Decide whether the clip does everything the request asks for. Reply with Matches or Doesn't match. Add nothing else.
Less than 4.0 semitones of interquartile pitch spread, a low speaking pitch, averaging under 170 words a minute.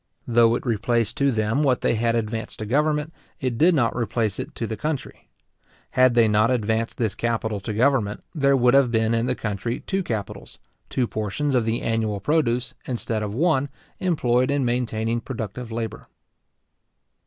Doesn't match